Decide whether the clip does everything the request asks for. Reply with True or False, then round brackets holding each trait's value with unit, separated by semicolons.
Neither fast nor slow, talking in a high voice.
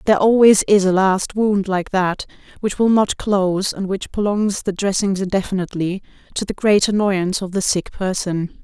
True (180 wpm; 195 Hz)